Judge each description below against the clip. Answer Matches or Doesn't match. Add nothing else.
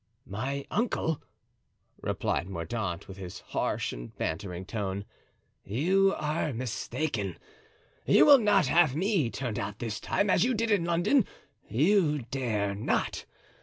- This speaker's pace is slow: Matches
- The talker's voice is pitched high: Doesn't match